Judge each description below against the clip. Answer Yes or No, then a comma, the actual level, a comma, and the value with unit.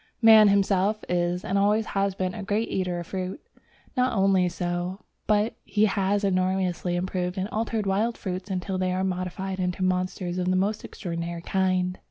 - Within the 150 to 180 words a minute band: Yes, average, 175 wpm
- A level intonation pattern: Yes, narrow, 1.8 semitones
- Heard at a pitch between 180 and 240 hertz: Yes, high, 190 Hz